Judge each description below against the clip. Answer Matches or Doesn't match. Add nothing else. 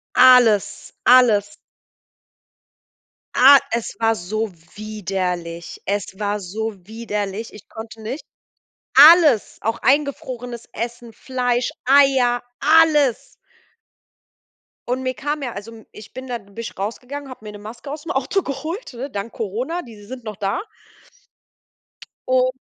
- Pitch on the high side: Matches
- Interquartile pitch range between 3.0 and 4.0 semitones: Matches